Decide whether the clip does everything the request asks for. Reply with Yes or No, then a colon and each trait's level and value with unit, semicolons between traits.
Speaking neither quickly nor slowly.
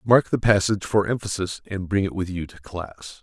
No: fast, 225 wpm